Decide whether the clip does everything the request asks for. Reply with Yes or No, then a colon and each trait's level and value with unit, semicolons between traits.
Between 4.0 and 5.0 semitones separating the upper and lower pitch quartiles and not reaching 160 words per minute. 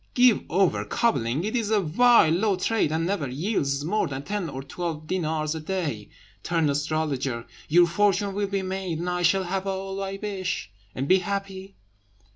No: average, 4.3 semitones; average, 180 wpm